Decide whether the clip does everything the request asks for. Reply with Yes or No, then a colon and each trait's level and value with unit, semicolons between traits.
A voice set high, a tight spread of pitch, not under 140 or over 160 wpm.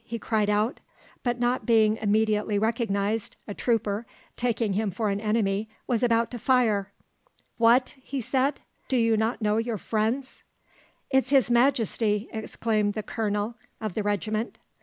Yes: high, 220 Hz; narrow, 2.2 semitones; average, 150 wpm